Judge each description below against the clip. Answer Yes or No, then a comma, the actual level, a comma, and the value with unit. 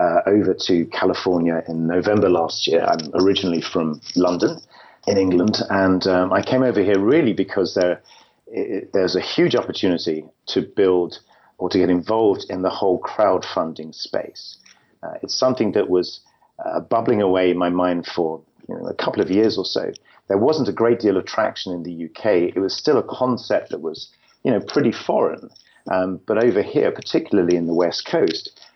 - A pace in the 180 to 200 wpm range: Yes, average, 185 wpm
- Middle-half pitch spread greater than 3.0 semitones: No, narrow, 2.4 semitones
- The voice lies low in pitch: Yes, very low, 90 Hz